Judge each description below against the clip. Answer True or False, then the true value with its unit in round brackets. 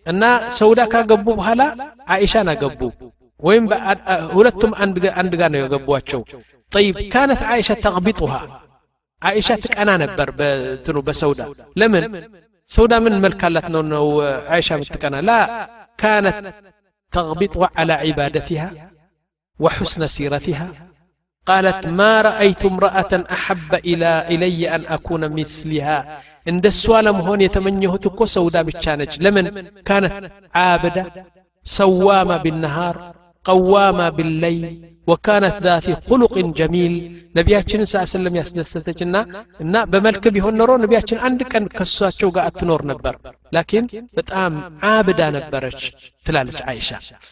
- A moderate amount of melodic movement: True (4.0 semitones)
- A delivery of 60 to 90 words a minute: False (110 wpm)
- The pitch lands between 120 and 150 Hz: False (180 Hz)